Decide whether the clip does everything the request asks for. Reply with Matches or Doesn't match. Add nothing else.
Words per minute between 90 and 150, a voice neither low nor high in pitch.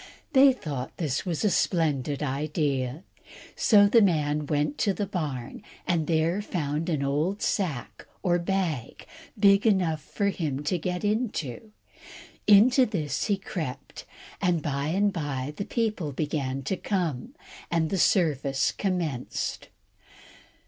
Matches